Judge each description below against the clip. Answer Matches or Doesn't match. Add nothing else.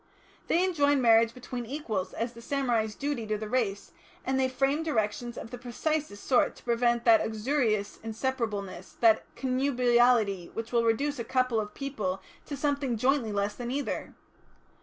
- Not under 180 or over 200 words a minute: Doesn't match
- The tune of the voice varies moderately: Matches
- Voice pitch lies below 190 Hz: Doesn't match